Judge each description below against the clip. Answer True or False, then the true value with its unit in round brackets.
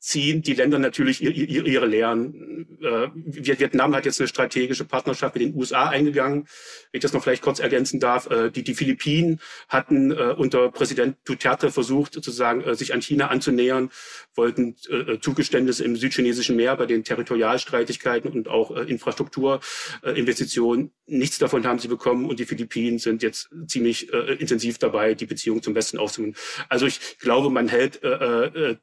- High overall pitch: False (130 Hz)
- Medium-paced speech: True (175 wpm)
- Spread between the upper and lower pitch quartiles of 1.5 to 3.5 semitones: False (4.2 semitones)